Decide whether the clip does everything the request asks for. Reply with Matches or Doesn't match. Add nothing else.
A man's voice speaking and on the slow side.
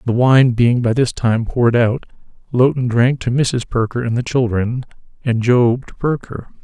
Doesn't match